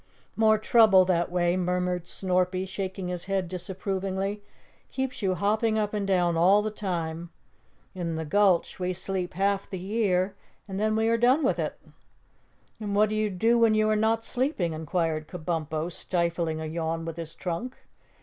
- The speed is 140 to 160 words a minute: No, average, 170 wpm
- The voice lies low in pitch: No, medium, 185 Hz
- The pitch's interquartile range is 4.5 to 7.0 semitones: No, average, 3.5 semitones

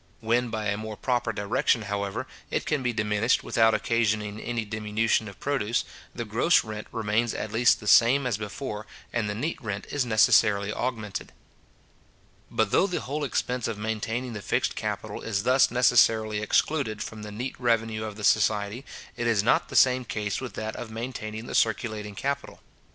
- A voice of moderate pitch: No, low, 110 Hz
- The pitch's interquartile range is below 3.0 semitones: Yes, narrow, 2.4 semitones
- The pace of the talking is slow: No, average, 180 wpm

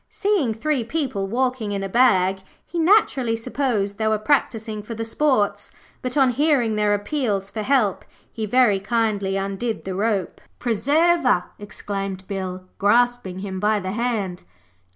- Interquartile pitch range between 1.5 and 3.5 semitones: No, average, 4.2 semitones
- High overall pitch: Yes, high, 220 Hz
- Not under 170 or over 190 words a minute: No, average, 150 wpm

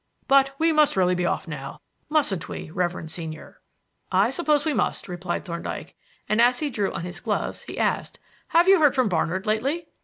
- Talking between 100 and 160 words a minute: No, average, 190 wpm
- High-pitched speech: Yes, high, 215 Hz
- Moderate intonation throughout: No, wide, 8.8 semitones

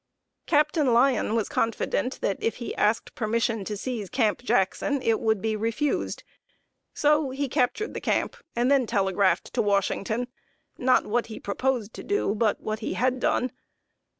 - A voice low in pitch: No, high, 230 Hz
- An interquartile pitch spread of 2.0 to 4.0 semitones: Yes, average, 3.4 semitones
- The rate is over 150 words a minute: Yes, average, 160 wpm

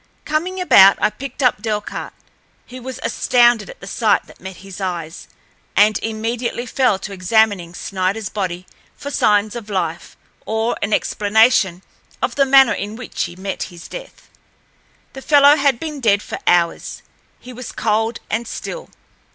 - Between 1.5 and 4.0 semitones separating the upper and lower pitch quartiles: No, average, 4.5 semitones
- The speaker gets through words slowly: No, average, 155 wpm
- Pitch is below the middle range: No, high, 220 Hz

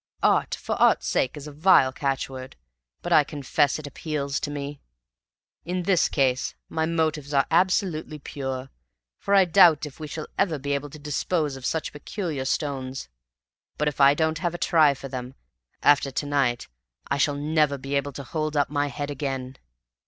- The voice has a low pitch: No, medium, 145 Hz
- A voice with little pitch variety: Yes, narrow, 2.3 semitones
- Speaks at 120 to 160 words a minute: No, average, 180 wpm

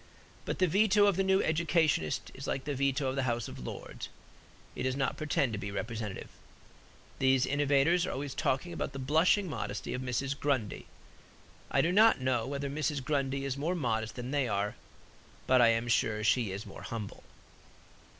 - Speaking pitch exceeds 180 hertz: No, low, 135 Hz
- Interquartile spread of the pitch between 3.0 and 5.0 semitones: Yes, average, 4.3 semitones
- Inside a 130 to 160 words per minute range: No, average, 185 wpm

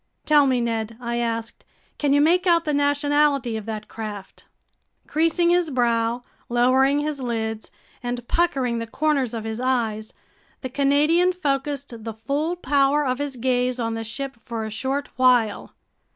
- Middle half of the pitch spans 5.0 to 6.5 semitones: No, average, 4.0 semitones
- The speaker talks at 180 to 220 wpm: No, average, 160 wpm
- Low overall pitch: No, very high, 255 Hz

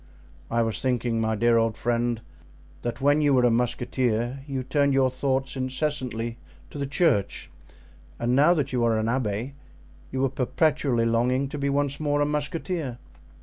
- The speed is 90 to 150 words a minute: No, average, 170 wpm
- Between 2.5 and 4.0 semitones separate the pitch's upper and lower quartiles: Yes, average, 3.2 semitones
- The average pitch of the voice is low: Yes, low, 130 Hz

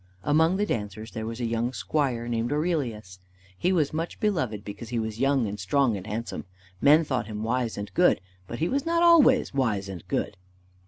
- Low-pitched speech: Yes, low, 120 Hz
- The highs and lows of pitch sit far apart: Yes, wide, 6.2 semitones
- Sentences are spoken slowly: No, average, 200 wpm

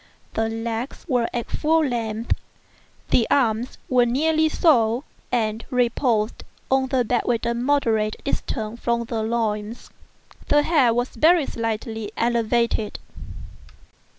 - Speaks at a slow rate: Yes, slow, 125 wpm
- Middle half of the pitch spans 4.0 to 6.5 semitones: No, average, 2.8 semitones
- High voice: Yes, high, 235 Hz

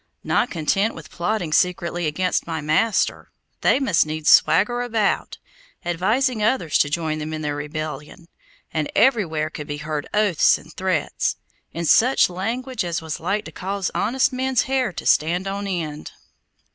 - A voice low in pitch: No, medium, 175 Hz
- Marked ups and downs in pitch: Yes, wide, 5.7 semitones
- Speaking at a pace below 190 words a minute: Yes, average, 160 wpm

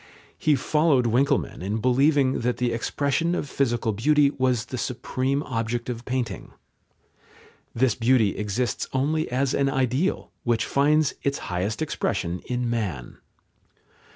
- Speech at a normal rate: No, slow, 130 wpm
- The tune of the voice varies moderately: Yes, average, 3.3 semitones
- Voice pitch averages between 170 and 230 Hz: No, low, 125 Hz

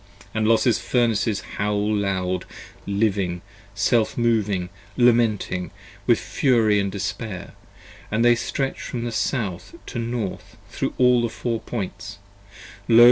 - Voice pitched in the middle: No, low, 110 Hz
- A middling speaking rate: No, slow, 120 wpm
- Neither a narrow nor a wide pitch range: Yes, average, 3.0 semitones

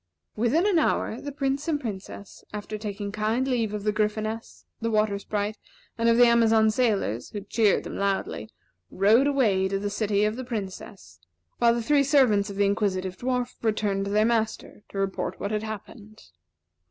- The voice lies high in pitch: Yes, high, 215 Hz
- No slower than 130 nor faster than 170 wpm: No, average, 180 wpm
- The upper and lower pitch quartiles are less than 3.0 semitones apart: Yes, narrow, 2.6 semitones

